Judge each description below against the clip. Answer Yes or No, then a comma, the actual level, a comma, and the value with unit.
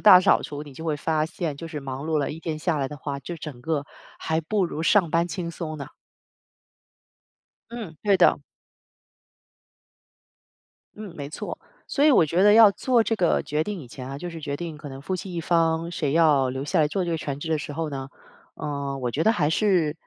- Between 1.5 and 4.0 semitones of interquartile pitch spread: Yes, average, 3.3 semitones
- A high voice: No, medium, 160 Hz